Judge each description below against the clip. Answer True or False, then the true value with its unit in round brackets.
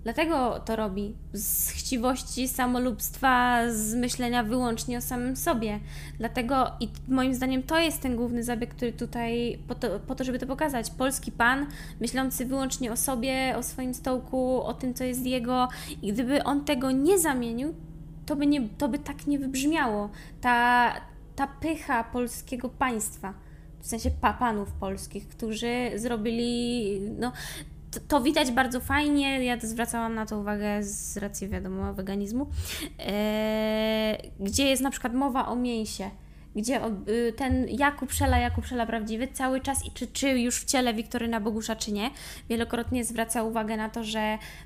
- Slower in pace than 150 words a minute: False (160 wpm)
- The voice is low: False (245 Hz)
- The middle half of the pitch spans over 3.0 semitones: False (2.7 semitones)